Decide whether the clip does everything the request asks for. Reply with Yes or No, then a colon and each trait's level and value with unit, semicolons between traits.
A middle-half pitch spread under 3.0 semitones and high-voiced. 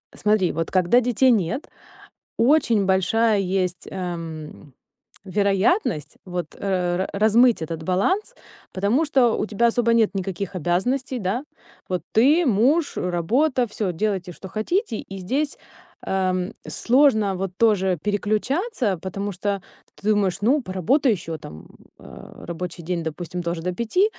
No: average, 4.9 semitones; high, 200 Hz